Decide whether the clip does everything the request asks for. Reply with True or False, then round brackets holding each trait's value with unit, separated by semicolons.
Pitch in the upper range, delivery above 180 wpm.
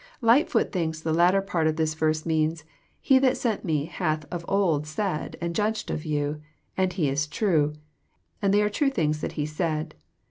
False (160 Hz; 200 wpm)